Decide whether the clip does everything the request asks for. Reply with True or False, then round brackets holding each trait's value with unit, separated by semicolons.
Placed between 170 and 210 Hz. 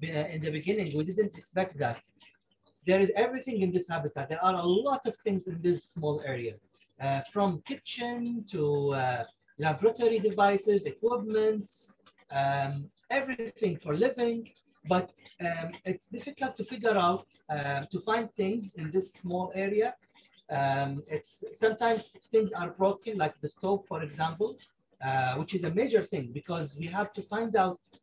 True (185 Hz)